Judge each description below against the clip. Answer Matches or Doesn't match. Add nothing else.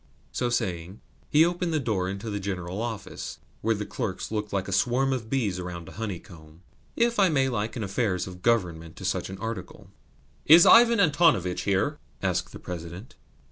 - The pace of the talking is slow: Doesn't match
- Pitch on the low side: Matches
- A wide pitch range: Matches